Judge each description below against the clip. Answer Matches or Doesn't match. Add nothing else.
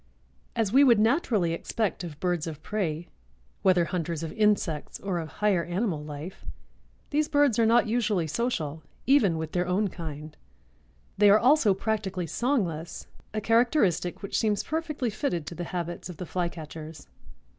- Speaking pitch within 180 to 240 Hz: Matches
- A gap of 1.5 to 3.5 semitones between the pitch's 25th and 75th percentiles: Doesn't match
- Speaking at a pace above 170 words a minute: Doesn't match